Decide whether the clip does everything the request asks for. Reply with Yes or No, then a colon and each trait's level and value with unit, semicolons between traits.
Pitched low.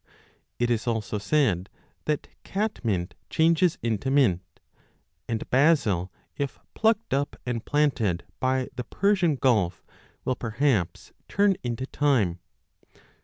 Yes: low, 125 Hz